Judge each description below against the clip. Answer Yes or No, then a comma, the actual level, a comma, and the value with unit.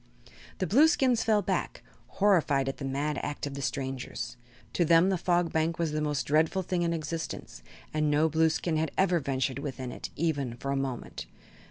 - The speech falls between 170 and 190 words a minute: Yes, average, 185 wpm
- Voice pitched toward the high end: No, medium, 155 Hz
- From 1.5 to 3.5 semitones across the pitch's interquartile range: No, average, 3.9 semitones